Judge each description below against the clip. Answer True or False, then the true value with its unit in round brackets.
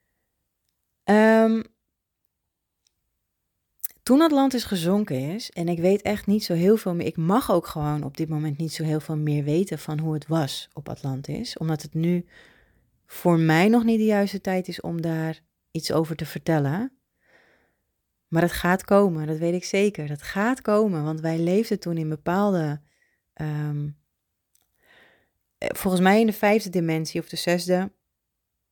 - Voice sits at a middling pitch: True (165 Hz)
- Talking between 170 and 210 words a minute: False (160 wpm)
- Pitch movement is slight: False (4.6 semitones)